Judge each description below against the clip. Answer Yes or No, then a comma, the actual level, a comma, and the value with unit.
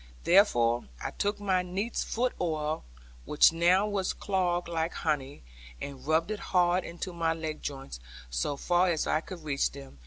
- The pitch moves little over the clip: No, average, 3.7 semitones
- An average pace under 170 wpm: Yes, average, 160 wpm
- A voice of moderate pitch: Yes, medium, 170 Hz